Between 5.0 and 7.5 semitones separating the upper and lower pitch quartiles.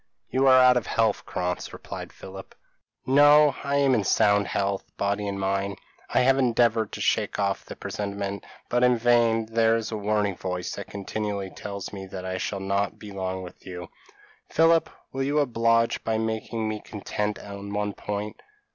No: average, 3.0 semitones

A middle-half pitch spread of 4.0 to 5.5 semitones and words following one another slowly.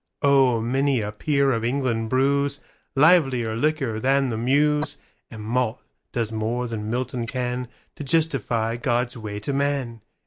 No: average, 3.4 semitones; slow, 130 wpm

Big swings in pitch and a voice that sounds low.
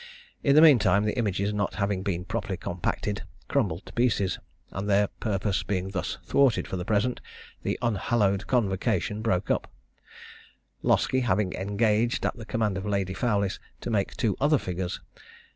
No: average, 3.2 semitones; low, 105 Hz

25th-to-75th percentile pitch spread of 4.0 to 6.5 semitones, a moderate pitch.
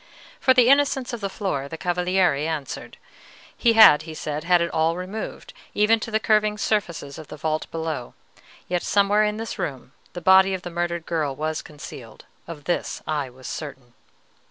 Yes: average, 5.3 semitones; medium, 175 Hz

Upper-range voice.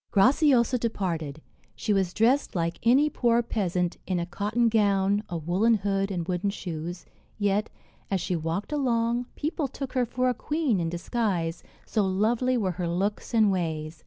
Yes: high, 200 Hz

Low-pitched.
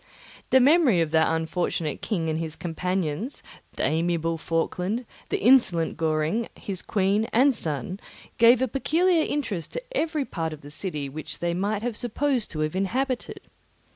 No: medium, 185 Hz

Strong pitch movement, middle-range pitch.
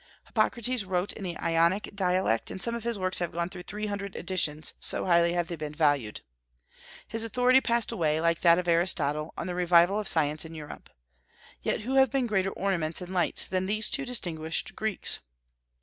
No: average, 4.1 semitones; medium, 180 Hz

